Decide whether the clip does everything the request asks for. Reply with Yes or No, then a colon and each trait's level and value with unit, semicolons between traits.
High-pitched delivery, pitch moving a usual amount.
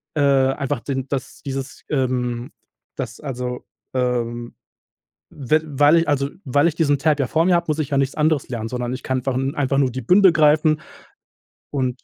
No: low, 135 Hz; average, 3.2 semitones